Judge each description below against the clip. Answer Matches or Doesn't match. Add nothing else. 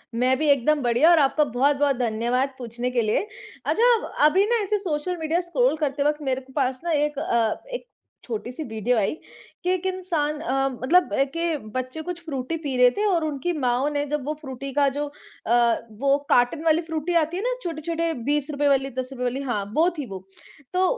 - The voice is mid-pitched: Doesn't match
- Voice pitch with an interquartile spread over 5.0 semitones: Doesn't match